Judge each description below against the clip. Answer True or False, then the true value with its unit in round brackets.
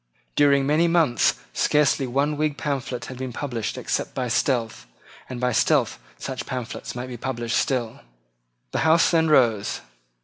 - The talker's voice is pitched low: True (130 Hz)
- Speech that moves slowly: False (150 wpm)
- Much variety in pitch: False (3.2 semitones)